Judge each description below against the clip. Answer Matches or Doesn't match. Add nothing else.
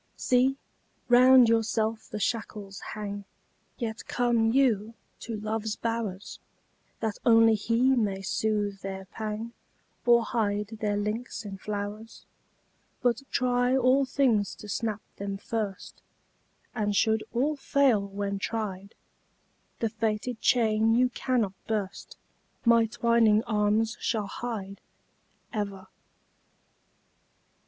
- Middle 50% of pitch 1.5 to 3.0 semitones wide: Matches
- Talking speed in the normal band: Doesn't match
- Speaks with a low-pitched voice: Doesn't match